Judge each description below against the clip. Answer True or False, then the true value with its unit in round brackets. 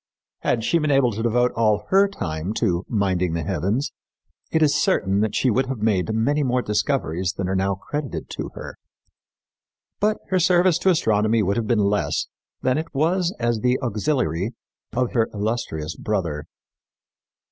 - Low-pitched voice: True (115 Hz)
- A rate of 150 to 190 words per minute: True (170 wpm)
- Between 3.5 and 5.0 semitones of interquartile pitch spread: False (5.6 semitones)